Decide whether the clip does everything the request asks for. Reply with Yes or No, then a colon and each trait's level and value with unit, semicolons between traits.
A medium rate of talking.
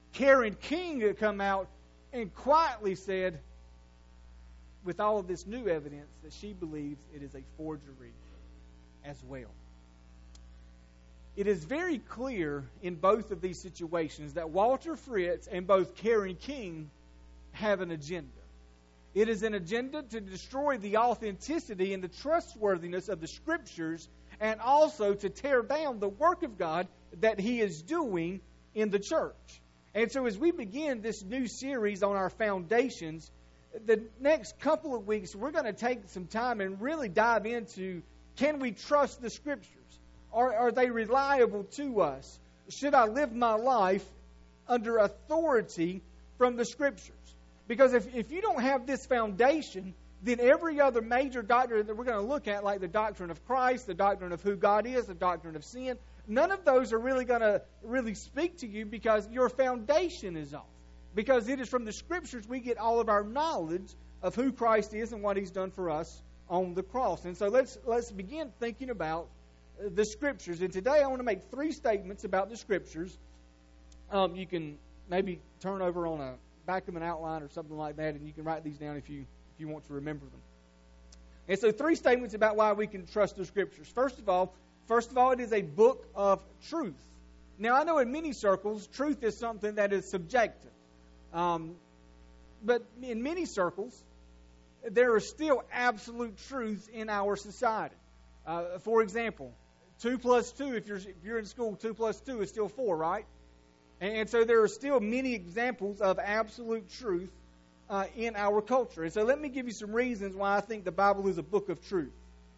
Yes: average, 185 wpm